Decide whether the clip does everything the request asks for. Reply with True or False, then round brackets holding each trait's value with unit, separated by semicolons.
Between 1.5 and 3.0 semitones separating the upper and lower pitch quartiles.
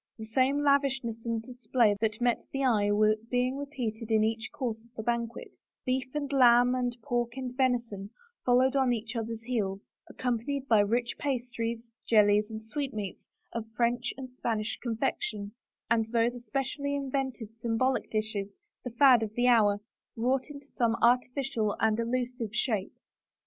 True (2.6 semitones)